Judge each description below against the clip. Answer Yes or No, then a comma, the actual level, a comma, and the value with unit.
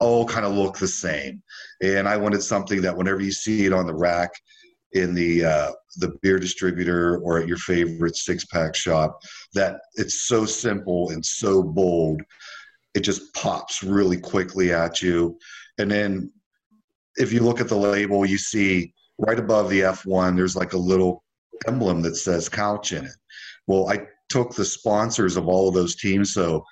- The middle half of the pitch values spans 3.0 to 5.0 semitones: No, narrow, 2.6 semitones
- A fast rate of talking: No, average, 180 wpm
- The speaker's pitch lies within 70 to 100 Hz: Yes, very low, 95 Hz